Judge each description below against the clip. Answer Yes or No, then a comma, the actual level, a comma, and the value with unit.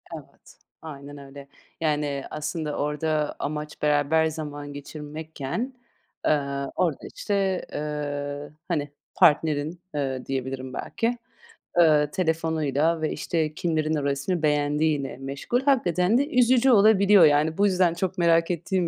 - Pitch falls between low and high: Yes, medium, 155 Hz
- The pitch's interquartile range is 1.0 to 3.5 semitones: Yes, average, 3.2 semitones